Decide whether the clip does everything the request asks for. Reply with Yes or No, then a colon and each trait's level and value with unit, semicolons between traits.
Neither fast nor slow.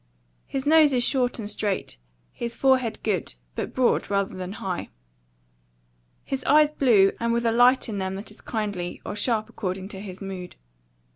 Yes: average, 170 wpm